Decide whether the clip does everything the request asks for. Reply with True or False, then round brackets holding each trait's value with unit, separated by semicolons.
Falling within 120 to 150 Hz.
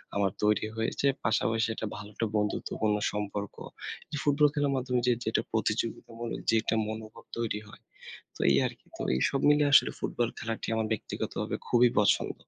False (110 Hz)